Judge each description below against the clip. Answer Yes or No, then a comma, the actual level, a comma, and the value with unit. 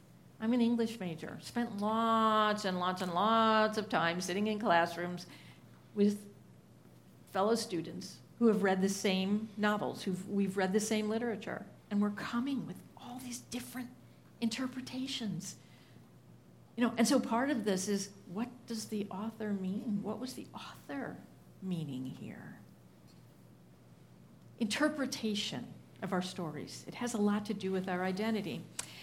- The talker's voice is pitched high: Yes, high, 210 Hz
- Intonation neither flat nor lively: Yes, average, 3.6 semitones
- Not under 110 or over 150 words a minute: Yes, average, 145 wpm